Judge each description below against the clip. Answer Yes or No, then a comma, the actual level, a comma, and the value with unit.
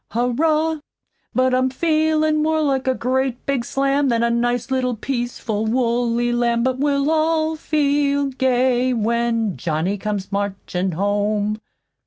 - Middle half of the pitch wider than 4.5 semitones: No, average, 3.5 semitones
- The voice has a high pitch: Yes, very high, 250 Hz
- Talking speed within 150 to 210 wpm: No, slow, 135 wpm